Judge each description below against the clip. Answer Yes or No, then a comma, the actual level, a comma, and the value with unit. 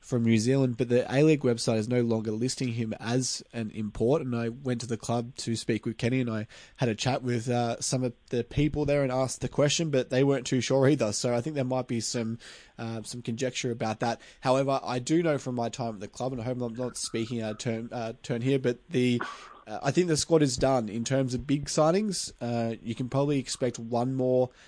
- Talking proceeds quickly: Yes, fast, 250 wpm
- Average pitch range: No, narrow, 2.3 semitones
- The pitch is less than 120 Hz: No, low, 125 Hz